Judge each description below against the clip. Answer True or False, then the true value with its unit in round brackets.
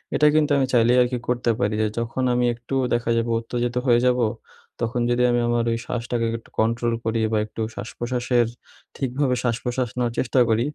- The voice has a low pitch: True (120 Hz)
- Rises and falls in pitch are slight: True (1.1 semitones)